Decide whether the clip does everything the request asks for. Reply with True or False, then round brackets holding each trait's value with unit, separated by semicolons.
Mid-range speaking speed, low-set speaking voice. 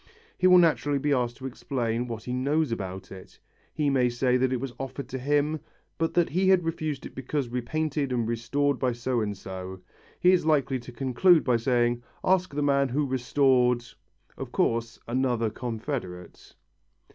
True (180 wpm; 130 Hz)